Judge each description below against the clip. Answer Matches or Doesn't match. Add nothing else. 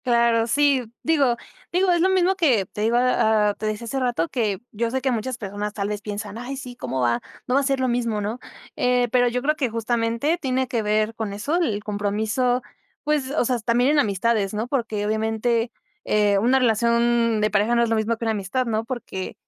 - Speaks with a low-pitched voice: Doesn't match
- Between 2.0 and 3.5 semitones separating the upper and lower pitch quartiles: Matches